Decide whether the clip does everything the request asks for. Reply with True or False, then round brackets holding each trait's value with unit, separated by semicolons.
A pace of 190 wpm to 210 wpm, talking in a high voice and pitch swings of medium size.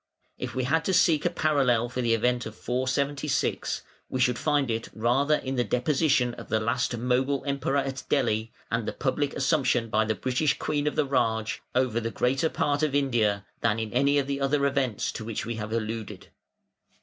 False (195 wpm; 130 Hz; 3.4 semitones)